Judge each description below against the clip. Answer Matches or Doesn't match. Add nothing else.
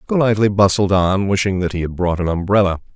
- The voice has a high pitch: Doesn't match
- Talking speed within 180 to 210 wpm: Matches